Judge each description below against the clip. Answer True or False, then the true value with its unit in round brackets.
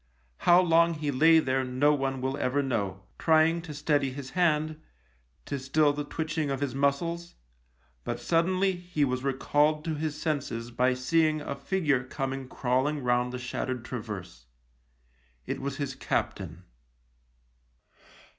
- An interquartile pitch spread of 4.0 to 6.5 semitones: False (3.5 semitones)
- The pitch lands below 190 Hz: True (140 Hz)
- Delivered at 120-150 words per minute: True (145 wpm)